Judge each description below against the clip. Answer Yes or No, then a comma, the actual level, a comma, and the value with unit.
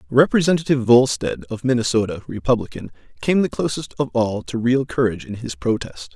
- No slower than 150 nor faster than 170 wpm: Yes, average, 155 wpm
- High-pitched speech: No, low, 125 Hz